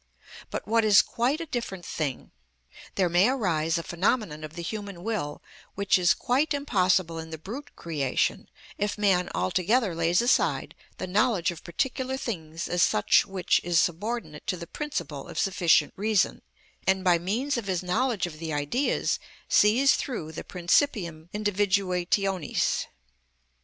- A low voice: No, medium, 185 Hz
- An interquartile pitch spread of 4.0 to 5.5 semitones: Yes, average, 4.8 semitones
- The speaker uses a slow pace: No, average, 150 wpm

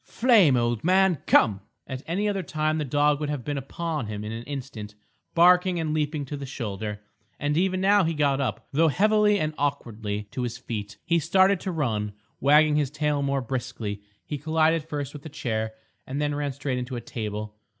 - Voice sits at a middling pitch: Yes, medium, 145 Hz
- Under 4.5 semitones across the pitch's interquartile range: No, average, 5.2 semitones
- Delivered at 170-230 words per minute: Yes, average, 200 wpm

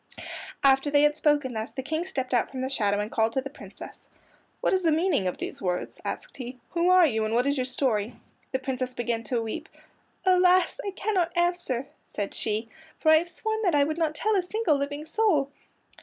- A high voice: Yes, very high, 280 Hz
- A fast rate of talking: Yes, fast, 215 wpm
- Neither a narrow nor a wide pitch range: No, wide, 5.9 semitones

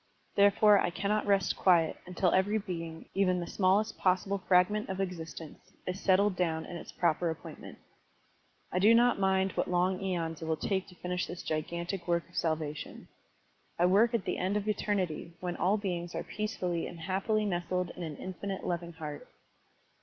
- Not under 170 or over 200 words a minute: Yes, average, 180 wpm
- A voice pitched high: No, medium, 180 Hz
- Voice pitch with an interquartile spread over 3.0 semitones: No, narrow, 2.5 semitones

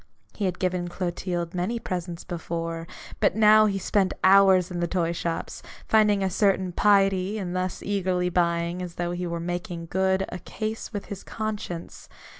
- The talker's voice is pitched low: No, medium, 185 Hz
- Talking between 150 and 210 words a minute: Yes, average, 170 wpm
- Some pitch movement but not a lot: No, narrow, 2.2 semitones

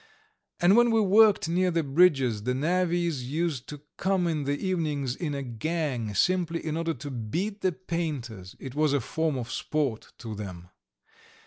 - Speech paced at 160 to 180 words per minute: Yes, average, 175 wpm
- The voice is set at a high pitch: No, medium, 155 Hz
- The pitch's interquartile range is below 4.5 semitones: No, wide, 5.5 semitones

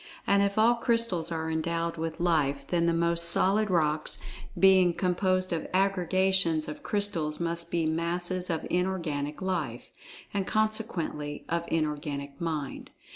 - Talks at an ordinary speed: No, slow, 130 wpm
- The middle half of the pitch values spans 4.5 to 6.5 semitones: No, average, 3.1 semitones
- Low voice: No, medium, 170 Hz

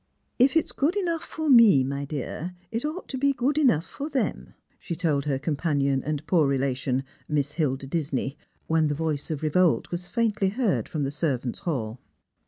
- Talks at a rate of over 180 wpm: Yes, average, 190 wpm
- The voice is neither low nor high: Yes, medium, 160 Hz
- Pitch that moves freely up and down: Yes, wide, 8.8 semitones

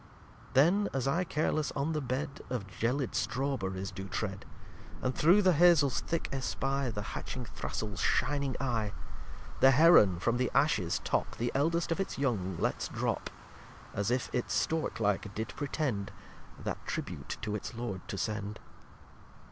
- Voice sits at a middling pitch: No, low, 130 Hz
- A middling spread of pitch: No, wide, 5.8 semitones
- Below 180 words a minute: Yes, average, 160 wpm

